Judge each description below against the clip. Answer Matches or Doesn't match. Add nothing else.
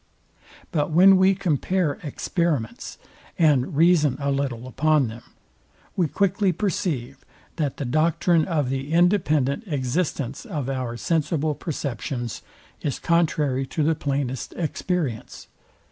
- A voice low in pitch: Doesn't match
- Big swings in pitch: Doesn't match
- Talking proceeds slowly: Matches